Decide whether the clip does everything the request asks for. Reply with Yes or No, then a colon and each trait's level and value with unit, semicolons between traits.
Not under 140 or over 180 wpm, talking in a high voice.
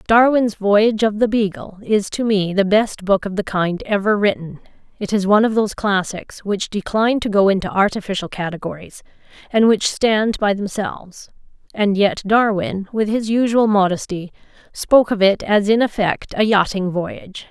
Yes: average, 170 wpm; high, 205 Hz